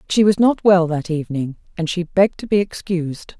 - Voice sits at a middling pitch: Yes, medium, 180 Hz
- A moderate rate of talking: No, fast, 210 wpm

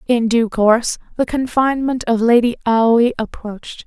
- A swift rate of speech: No, average, 140 wpm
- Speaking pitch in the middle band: No, high, 235 Hz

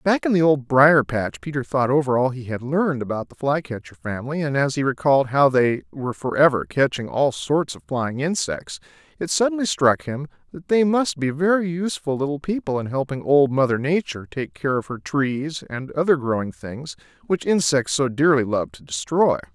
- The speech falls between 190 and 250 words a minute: Yes, average, 195 wpm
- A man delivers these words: Yes, male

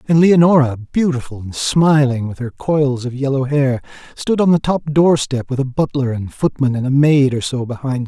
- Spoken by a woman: No, male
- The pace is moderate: No, fast, 210 wpm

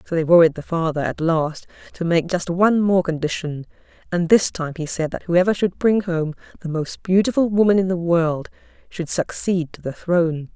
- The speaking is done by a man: No, female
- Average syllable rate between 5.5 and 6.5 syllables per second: No, 5.1 syllables/s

